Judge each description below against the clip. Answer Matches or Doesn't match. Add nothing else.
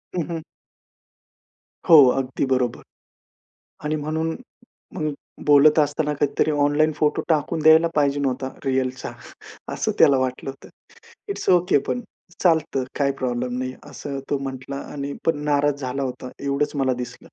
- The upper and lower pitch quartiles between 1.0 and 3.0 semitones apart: Matches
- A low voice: Doesn't match